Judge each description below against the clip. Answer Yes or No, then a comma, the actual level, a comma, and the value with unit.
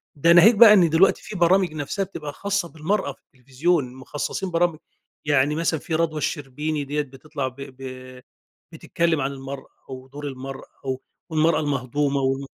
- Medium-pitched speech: Yes, medium, 150 Hz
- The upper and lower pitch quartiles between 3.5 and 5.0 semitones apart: Yes, average, 3.9 semitones